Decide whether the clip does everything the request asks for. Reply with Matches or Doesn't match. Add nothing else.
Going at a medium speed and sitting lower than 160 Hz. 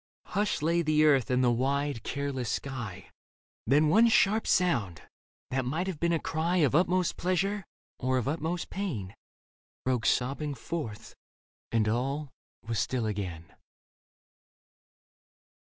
Doesn't match